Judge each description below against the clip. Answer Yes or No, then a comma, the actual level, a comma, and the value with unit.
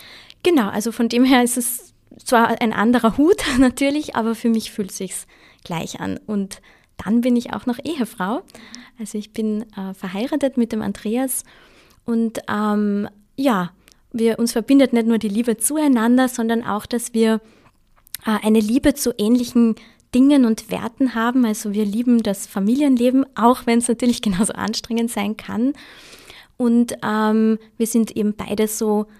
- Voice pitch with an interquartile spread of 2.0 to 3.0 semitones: Yes, narrow, 2.4 semitones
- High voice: Yes, high, 230 Hz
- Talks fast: No, average, 160 wpm